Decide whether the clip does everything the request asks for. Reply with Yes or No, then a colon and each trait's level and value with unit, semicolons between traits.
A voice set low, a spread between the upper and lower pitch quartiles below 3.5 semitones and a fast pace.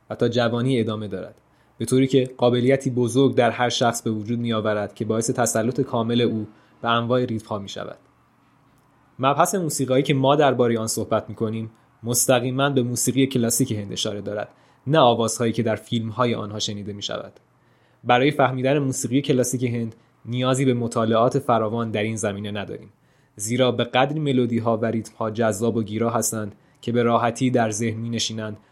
Yes: low, 120 Hz; narrow, 2.5 semitones; fast, 170 wpm